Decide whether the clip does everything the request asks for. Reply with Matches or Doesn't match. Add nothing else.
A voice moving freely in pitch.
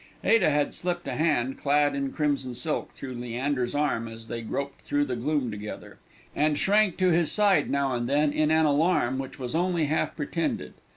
Doesn't match